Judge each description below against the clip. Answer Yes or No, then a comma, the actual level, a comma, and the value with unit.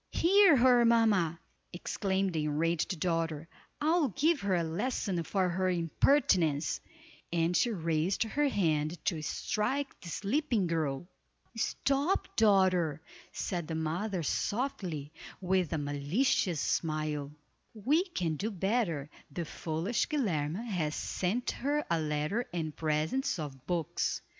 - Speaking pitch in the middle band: Yes, medium, 180 Hz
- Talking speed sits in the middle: No, slow, 125 wpm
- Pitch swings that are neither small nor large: No, wide, 6.5 semitones